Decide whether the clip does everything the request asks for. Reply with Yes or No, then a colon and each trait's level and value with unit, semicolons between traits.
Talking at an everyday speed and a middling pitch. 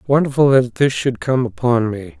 No: average, 190 wpm; low, 130 Hz